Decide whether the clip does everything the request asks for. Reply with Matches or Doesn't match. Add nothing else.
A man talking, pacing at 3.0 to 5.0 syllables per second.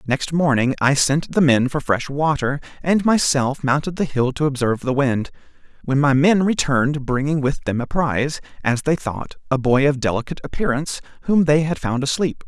Doesn't match